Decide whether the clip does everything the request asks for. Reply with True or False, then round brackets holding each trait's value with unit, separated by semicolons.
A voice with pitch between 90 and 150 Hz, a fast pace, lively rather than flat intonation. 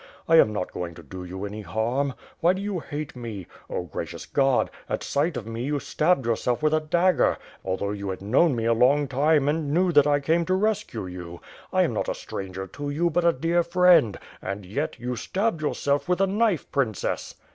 True (140 Hz; 215 wpm; 7.7 semitones)